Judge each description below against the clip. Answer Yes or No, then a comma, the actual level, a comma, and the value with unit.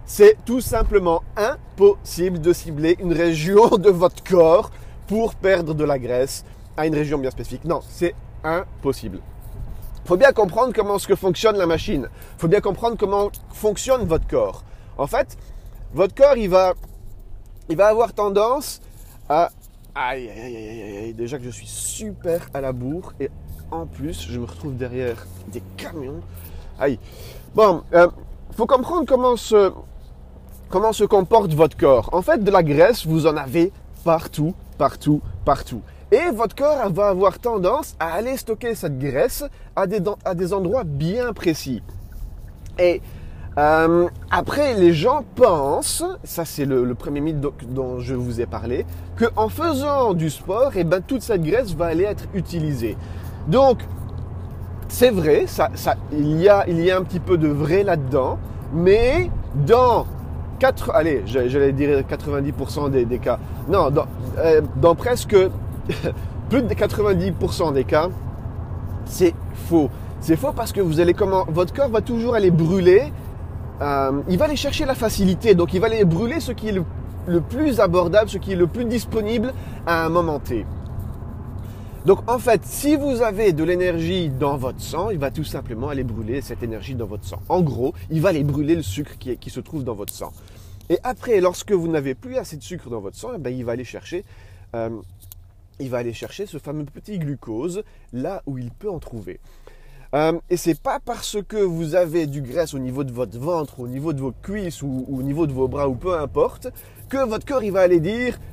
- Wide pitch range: Yes, wide, 8.5 semitones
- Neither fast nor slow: Yes, average, 185 wpm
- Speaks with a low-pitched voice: No, medium, 165 Hz